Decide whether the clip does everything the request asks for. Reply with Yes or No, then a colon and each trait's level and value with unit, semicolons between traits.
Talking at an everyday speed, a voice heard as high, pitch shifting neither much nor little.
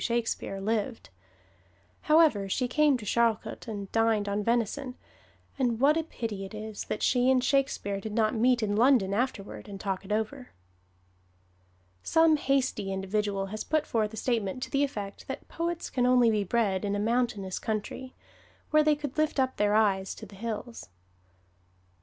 Yes: average, 170 wpm; high, 225 Hz; average, 4.1 semitones